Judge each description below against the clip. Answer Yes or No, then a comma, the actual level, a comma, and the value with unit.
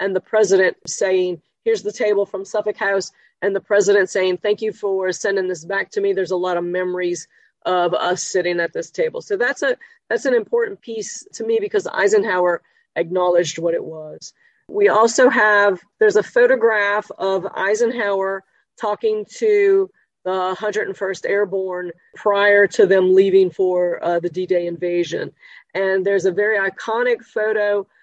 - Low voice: No, high, 200 Hz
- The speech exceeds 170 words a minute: No, average, 165 wpm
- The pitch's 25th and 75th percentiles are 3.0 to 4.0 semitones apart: Yes, average, 3.5 semitones